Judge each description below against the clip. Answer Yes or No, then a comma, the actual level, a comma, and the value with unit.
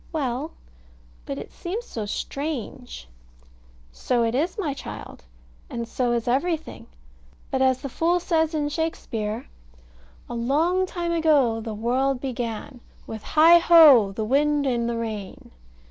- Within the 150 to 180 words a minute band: No, average, 140 wpm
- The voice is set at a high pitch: Yes, very high, 265 Hz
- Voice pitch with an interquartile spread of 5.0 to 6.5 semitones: Yes, wide, 5.4 semitones